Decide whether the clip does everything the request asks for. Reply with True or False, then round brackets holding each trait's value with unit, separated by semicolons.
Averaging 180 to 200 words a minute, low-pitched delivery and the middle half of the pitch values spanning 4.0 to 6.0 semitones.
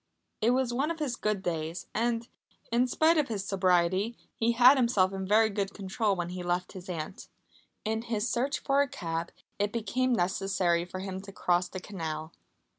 False (190 wpm; 200 Hz; 4.7 semitones)